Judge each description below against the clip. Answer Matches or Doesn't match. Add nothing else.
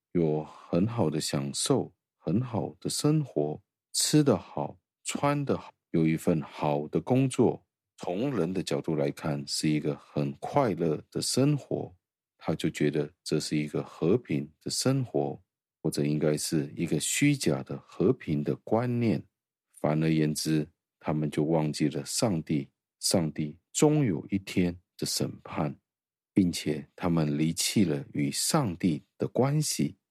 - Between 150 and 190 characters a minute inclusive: Doesn't match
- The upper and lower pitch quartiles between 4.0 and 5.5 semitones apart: Doesn't match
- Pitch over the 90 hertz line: Doesn't match